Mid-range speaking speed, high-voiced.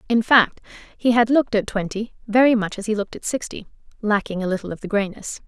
No: fast, 220 wpm; high, 215 Hz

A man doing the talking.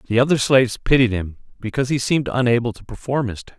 Yes: male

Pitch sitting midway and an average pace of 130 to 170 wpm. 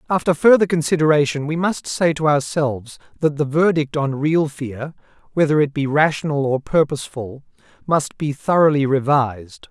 Yes: medium, 150 Hz; average, 150 wpm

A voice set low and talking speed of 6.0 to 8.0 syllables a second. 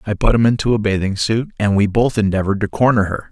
Yes: low, 105 Hz; 6.5 syllables/s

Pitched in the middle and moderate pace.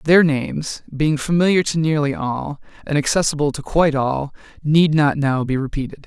Yes: medium, 150 Hz; average, 170 wpm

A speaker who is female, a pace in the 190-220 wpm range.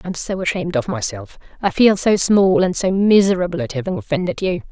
Yes: female; fast, 205 wpm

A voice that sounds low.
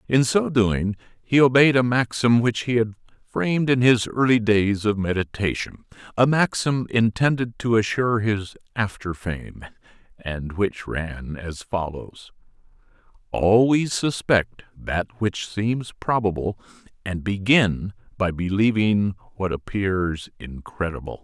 Yes: low, 105 Hz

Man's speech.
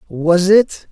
Yes: male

